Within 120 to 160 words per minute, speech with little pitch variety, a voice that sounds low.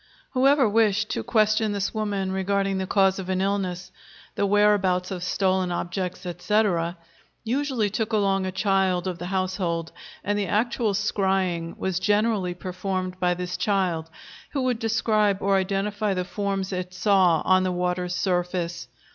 No: average, 155 wpm; narrow, 2.3 semitones; high, 190 Hz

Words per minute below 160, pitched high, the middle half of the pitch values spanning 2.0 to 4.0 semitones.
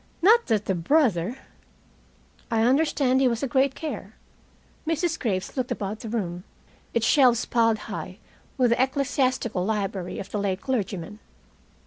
No: average, 150 wpm; high, 235 Hz; average, 4.8 semitones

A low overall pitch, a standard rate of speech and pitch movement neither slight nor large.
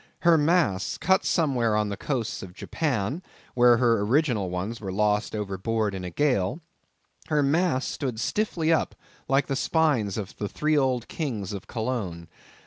No: low, 120 Hz; average, 150 wpm; wide, 6.5 semitones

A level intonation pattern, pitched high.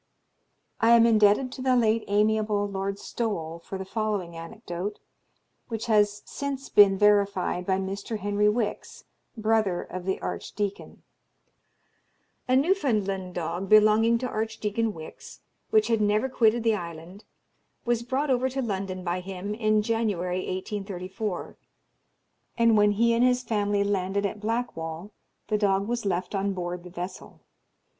No: average, 3.0 semitones; high, 210 Hz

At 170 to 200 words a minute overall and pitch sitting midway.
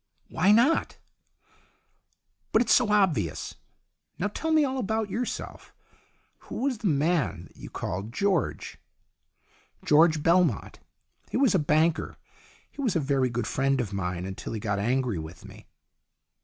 No: average, 155 wpm; medium, 155 Hz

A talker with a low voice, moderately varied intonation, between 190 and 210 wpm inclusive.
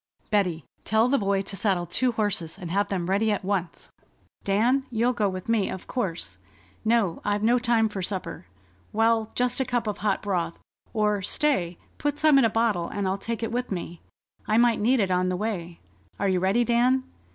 No: high, 210 Hz; average, 3.8 semitones; average, 200 wpm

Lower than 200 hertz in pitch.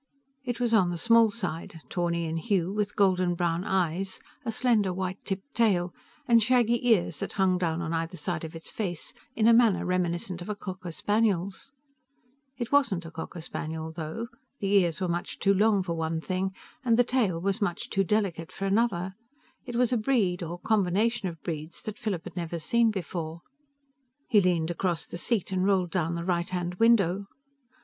Yes: medium, 185 Hz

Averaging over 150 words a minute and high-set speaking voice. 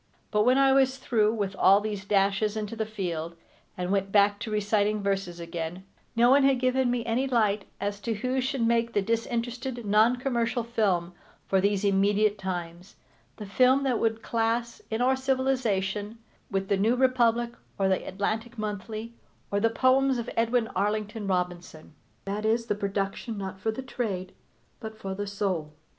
Yes: average, 175 wpm; high, 215 Hz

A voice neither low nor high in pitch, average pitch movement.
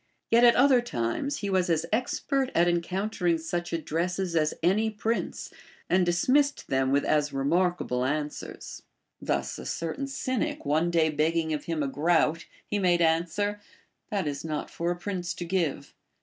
Yes: medium, 175 Hz; average, 4.4 semitones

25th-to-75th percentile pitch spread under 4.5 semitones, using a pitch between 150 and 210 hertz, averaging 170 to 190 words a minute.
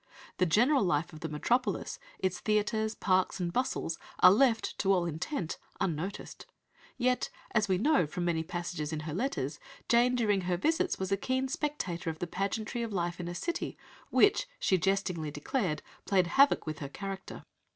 No: average, 5.2 semitones; high, 190 Hz; average, 175 wpm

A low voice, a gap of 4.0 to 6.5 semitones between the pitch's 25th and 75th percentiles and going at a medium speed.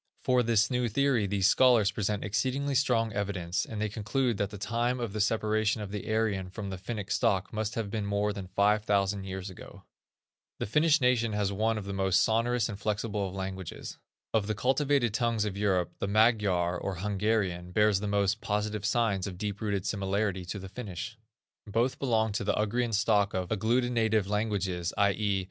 No: low, 105 Hz; narrow, 2.4 semitones; average, 190 wpm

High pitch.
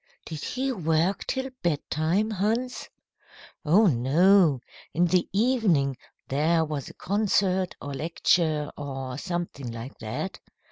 No: medium, 170 Hz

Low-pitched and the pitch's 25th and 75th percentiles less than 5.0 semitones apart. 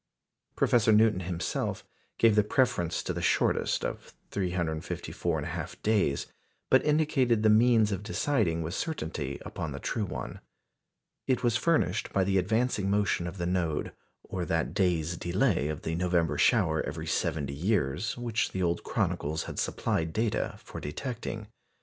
No: very low, 95 Hz; average, 5.3 semitones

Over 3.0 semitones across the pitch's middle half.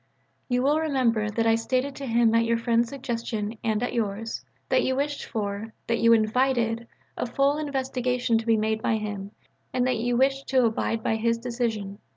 No: narrow, 2.4 semitones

